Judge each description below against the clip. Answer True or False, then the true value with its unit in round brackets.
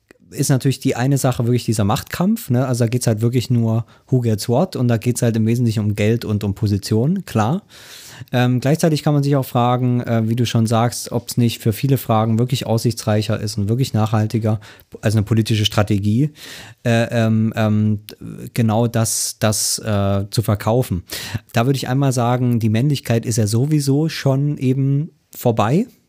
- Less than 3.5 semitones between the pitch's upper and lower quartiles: True (2.8 semitones)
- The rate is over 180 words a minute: True (190 wpm)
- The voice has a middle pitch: False (120 Hz)